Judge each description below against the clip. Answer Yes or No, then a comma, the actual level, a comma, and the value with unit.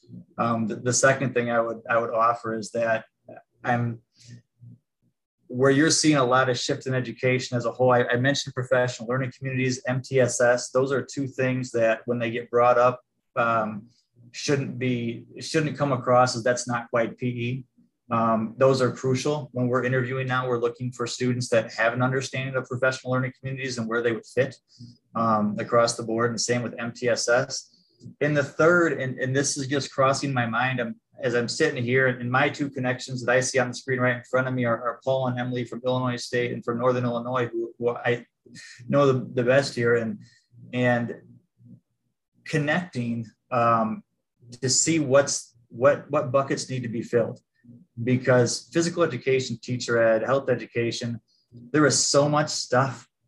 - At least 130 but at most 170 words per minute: No, average, 185 wpm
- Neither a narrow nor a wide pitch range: No, narrow, 1.8 semitones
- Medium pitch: No, low, 125 Hz